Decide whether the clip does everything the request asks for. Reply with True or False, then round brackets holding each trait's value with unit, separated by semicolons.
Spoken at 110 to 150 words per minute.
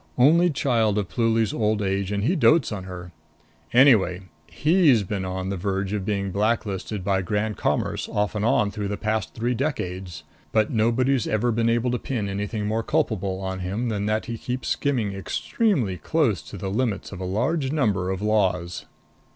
False (185 wpm)